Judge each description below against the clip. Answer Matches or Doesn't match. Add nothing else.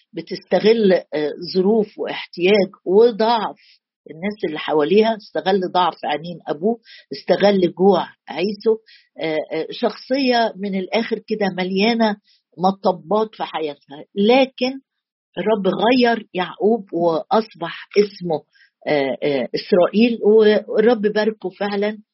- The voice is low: Doesn't match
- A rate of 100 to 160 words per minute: Doesn't match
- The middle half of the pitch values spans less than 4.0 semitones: Matches